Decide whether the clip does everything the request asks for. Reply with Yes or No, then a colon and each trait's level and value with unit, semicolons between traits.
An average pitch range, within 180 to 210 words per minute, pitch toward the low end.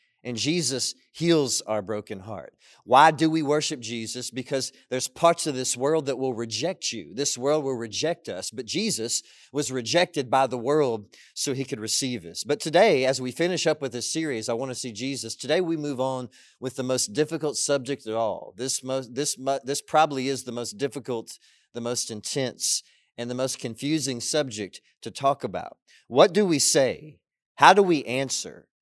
Yes: average, 3.5 semitones; average, 190 wpm; low, 130 Hz